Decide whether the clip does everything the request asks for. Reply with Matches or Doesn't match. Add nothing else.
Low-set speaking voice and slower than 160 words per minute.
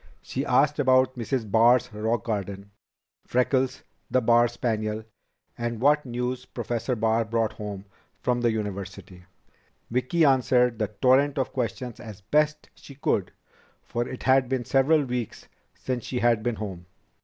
Matches